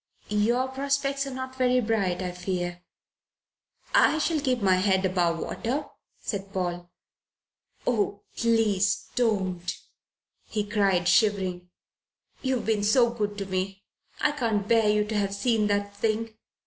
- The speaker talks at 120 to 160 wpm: Yes, average, 140 wpm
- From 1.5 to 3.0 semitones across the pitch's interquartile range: No, average, 4.0 semitones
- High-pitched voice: Yes, high, 210 Hz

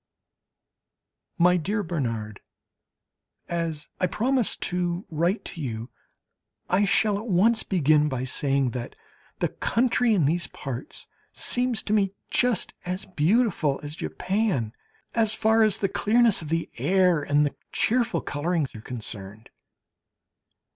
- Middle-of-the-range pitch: Yes, medium, 175 Hz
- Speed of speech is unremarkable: No, slow, 130 wpm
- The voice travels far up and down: Yes, wide, 6.5 semitones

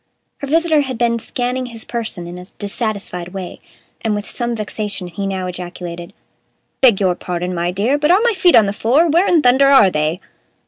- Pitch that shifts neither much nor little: No, wide, 6.3 semitones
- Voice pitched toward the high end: Yes, high, 215 Hz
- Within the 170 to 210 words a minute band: Yes, average, 200 wpm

